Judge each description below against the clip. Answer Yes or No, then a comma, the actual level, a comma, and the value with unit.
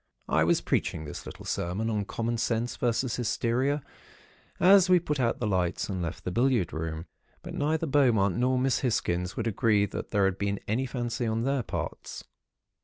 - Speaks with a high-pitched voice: No, low, 115 Hz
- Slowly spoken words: No, average, 180 wpm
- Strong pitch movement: No, average, 4.7 semitones